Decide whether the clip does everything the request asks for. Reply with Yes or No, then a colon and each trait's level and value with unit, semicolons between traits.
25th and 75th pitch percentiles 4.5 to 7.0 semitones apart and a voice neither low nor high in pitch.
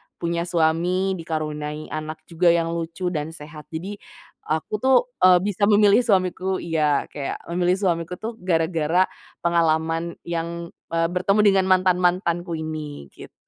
No: narrow, 2.4 semitones; medium, 170 Hz